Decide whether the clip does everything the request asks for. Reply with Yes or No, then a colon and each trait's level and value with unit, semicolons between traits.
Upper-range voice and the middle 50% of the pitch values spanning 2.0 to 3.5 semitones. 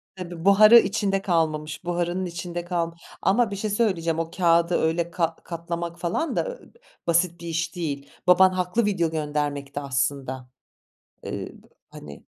No: medium, 170 Hz; narrow, 2.5 semitones